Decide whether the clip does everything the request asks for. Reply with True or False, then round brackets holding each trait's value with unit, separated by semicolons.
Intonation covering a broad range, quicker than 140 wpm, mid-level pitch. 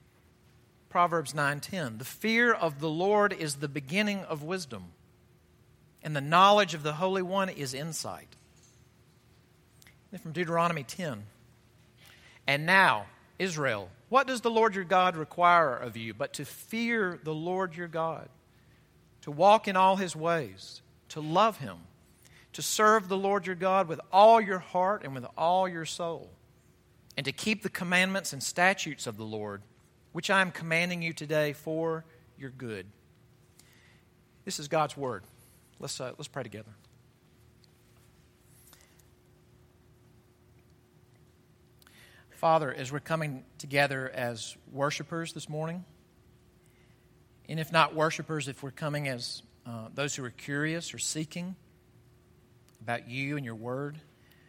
False (6.4 semitones; 135 wpm; 155 Hz)